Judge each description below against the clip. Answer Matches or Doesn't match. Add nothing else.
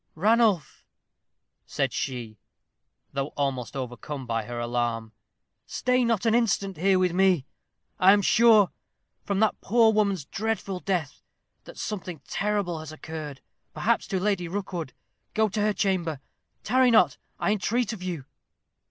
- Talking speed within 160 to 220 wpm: Doesn't match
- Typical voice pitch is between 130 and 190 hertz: Matches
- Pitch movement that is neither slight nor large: Doesn't match